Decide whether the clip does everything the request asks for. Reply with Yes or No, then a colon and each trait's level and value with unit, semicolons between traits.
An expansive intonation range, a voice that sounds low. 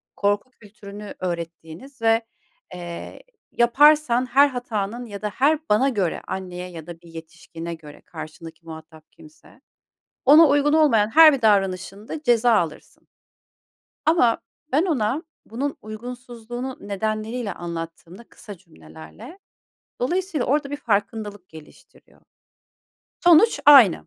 No: wide, 7.1 semitones; high, 215 Hz